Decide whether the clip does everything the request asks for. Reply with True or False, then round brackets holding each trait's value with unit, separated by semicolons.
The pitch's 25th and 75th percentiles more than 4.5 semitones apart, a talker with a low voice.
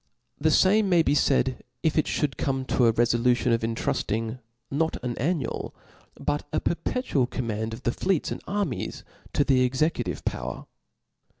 True (5.0 semitones; 130 Hz)